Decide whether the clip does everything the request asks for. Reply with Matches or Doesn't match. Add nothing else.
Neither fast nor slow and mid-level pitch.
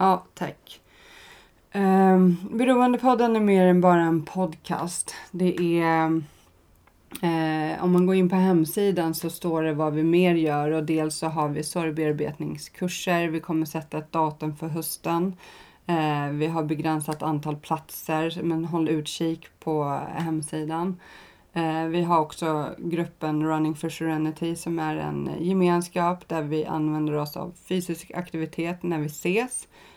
Matches